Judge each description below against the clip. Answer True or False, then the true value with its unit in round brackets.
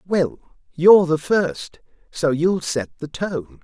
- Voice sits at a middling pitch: True (160 Hz)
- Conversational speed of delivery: True (150 wpm)